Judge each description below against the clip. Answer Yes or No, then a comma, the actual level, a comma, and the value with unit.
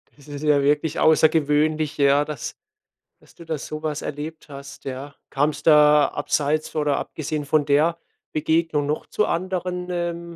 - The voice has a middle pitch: Yes, medium, 150 Hz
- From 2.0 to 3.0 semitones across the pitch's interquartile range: No, narrow, 1.6 semitones